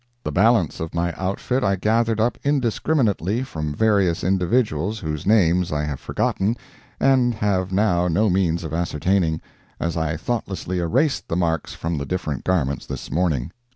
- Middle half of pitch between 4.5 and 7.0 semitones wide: Yes, average, 5.1 semitones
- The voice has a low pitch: Yes, very low, 90 Hz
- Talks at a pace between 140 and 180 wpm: Yes, average, 155 wpm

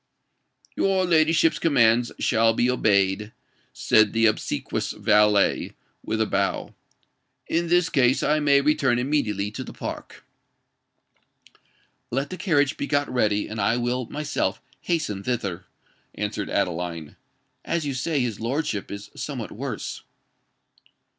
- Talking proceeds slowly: Yes, slow, 130 wpm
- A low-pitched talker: Yes, low, 120 Hz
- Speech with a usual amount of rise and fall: No, wide, 5.9 semitones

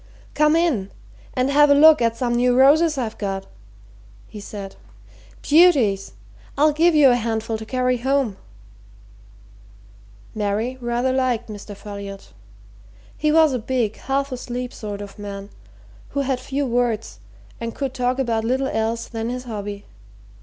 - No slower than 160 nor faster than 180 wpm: No, average, 145 wpm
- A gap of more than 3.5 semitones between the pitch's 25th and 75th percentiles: Yes, average, 4.0 semitones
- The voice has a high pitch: Yes, high, 245 Hz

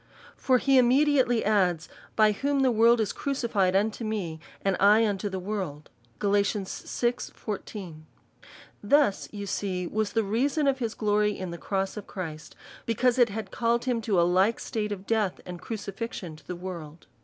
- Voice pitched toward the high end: Yes, high, 210 Hz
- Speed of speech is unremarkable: Yes, average, 175 wpm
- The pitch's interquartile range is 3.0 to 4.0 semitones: Yes, average, 3.6 semitones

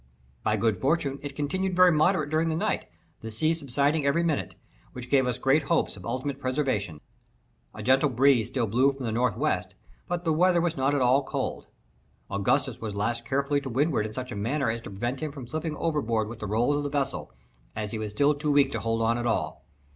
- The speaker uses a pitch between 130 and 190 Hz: Yes, low, 135 Hz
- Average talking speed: No, fast, 225 wpm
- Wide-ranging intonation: No, average, 4.4 semitones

